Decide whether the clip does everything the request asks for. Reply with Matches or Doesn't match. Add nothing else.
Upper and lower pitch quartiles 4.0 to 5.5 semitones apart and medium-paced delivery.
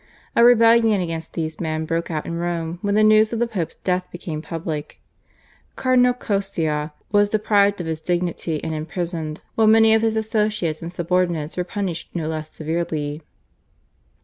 Matches